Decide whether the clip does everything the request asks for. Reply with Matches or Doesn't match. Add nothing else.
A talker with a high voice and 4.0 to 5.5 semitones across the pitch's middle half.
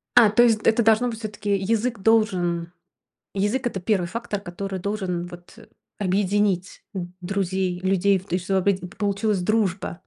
Doesn't match